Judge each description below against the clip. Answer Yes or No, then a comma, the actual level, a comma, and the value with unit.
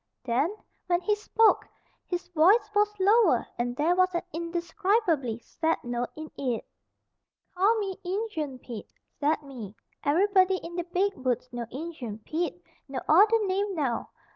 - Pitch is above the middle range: Yes, very high, 340 Hz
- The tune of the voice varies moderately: No, wide, 6.8 semitones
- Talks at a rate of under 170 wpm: Yes, average, 145 wpm